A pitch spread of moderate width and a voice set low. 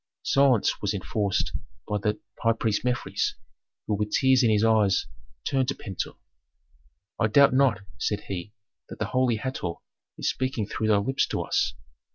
Yes: average, 3.9 semitones; low, 110 Hz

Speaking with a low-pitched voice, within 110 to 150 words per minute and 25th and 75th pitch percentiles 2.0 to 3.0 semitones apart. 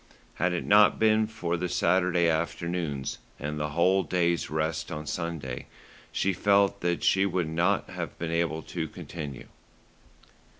Yes: very low, 85 Hz; average, 145 wpm; narrow, 2.6 semitones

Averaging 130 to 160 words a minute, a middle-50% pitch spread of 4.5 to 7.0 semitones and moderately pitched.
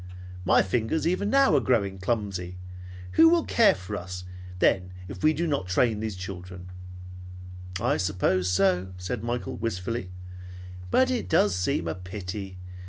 No: average, 155 wpm; average, 5.0 semitones; low, 100 Hz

